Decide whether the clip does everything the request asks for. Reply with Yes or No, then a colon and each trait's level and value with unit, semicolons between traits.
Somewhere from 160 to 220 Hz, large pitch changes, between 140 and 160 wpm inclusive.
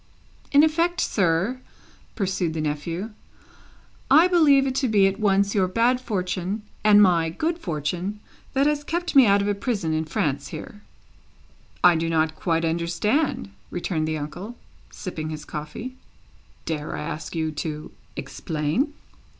Yes: medium, 185 Hz; wide, 7.5 semitones; average, 150 wpm